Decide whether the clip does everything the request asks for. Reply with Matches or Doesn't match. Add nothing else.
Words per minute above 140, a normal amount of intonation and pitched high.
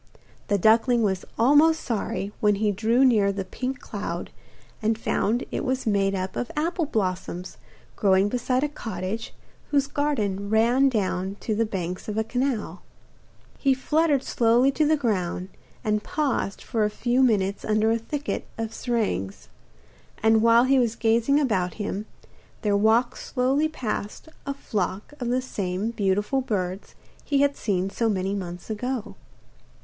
Matches